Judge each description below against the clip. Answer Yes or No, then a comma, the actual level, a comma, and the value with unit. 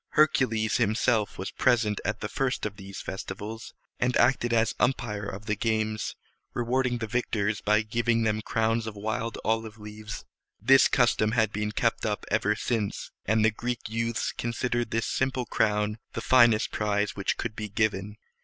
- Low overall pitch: Yes, low, 110 Hz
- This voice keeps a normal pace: Yes, average, 165 wpm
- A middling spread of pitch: No, narrow, 1.9 semitones